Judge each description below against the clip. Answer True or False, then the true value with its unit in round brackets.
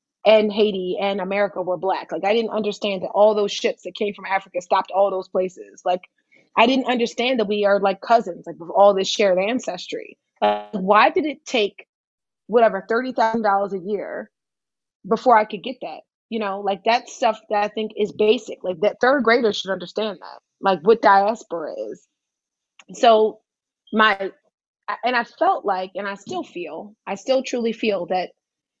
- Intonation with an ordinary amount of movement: True (3.0 semitones)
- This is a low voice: False (210 Hz)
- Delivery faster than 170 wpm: True (180 wpm)